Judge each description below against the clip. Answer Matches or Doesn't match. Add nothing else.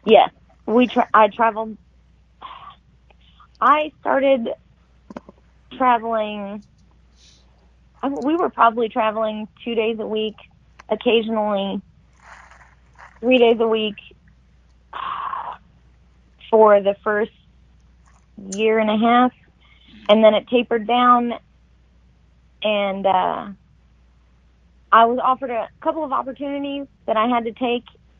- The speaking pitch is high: Matches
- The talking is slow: Matches